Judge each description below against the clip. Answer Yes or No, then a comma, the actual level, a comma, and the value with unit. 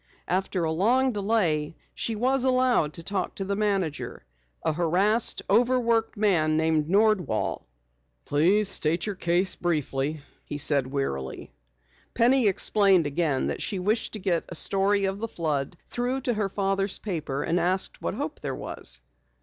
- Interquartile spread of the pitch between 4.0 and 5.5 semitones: Yes, average, 5.0 semitones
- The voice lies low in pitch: No, high, 190 Hz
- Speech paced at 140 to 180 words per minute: Yes, average, 160 wpm